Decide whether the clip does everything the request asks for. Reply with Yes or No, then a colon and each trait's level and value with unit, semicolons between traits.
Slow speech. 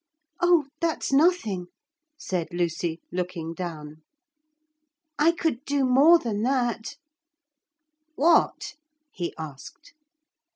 Yes: slow, 90 wpm